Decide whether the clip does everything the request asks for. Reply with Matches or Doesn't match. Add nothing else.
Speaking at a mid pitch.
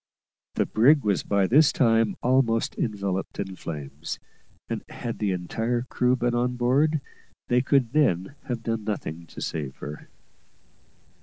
Doesn't match